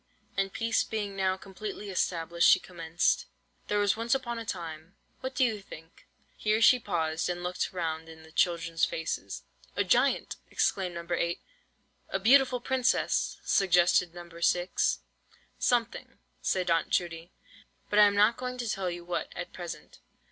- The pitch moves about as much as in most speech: Yes, average, 4.0 semitones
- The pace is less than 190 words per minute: Yes, average, 155 wpm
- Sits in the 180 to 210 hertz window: Yes, medium, 185 Hz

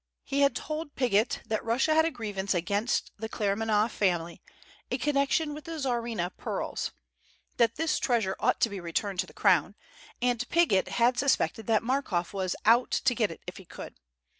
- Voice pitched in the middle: No, high, 230 Hz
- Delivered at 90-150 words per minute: No, average, 180 wpm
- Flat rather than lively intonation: No, average, 5.2 semitones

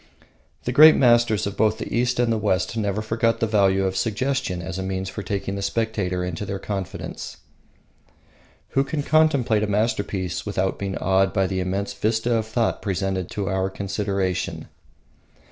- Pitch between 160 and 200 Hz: No, low, 100 Hz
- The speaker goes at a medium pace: Yes, average, 170 wpm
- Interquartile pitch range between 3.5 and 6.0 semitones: No, average, 3.1 semitones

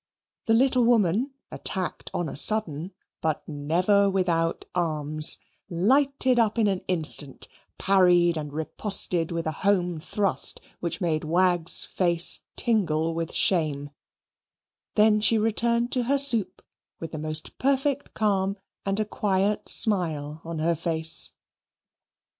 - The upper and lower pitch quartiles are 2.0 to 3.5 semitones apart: No, average, 4.9 semitones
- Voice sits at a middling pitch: Yes, medium, 180 Hz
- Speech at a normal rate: No, slow, 130 wpm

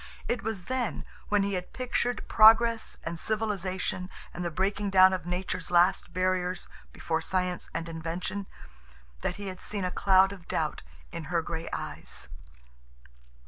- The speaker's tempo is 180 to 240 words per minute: No, average, 150 wpm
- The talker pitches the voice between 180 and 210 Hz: Yes, medium, 185 Hz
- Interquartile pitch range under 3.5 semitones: Yes, narrow, 2.5 semitones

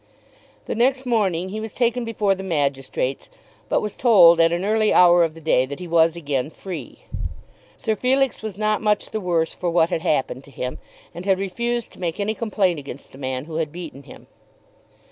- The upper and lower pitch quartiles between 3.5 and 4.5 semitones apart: No, average, 5.1 semitones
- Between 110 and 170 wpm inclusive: No, fast, 205 wpm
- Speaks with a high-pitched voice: No, medium, 180 Hz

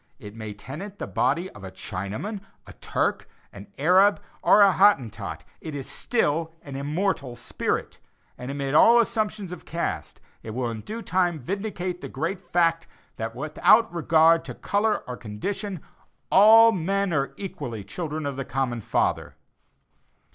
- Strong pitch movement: Yes, wide, 7.5 semitones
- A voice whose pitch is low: No, medium, 165 Hz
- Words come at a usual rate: Yes, average, 155 wpm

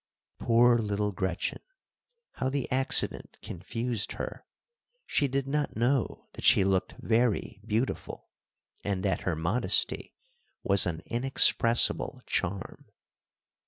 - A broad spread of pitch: No, average, 4.4 semitones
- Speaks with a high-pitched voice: No, low, 115 Hz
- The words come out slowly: Yes, slow, 110 wpm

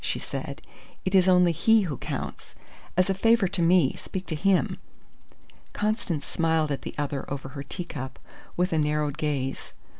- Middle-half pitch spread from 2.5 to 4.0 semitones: No, average, 4.4 semitones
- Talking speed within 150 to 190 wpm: Yes, average, 170 wpm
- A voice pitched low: No, medium, 165 Hz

